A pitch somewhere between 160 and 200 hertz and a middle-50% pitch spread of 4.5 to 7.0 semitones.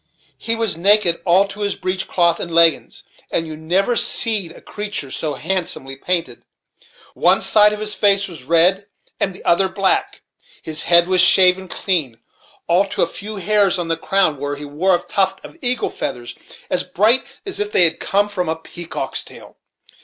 No: medium, 185 Hz; average, 3.5 semitones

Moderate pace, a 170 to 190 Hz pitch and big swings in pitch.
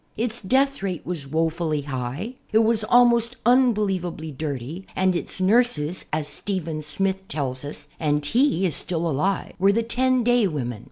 Yes: average, 165 wpm; medium, 185 Hz; wide, 7.0 semitones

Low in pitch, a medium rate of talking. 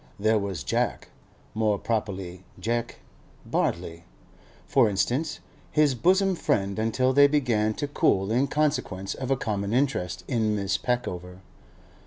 No: low, 110 Hz; slow, 120 wpm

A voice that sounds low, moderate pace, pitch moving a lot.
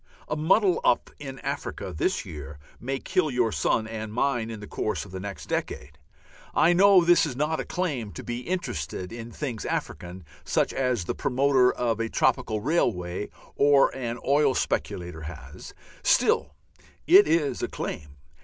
Yes: low, 125 Hz; average, 165 wpm; wide, 6.0 semitones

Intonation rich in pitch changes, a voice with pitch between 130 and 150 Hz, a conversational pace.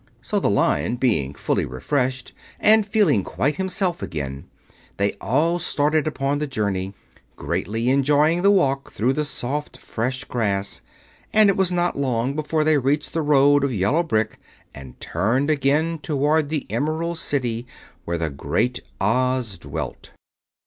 Yes: wide, 5.7 semitones; low, 135 Hz; average, 150 wpm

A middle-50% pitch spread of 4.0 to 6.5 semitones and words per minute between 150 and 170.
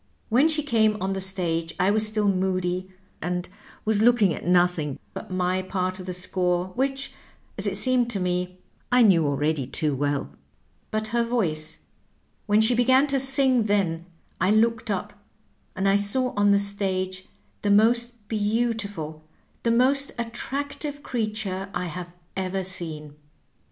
Yes: average, 4.5 semitones; average, 155 wpm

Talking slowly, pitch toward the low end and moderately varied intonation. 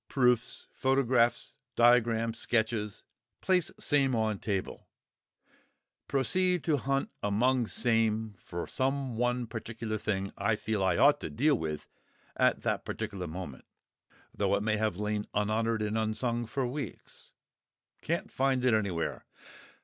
Yes: slow, 130 wpm; low, 115 Hz; average, 3.4 semitones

